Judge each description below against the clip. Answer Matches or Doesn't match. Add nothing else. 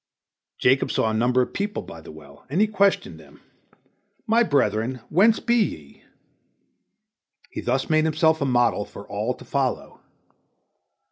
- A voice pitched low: Matches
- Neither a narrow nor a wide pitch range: Doesn't match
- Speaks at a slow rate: Doesn't match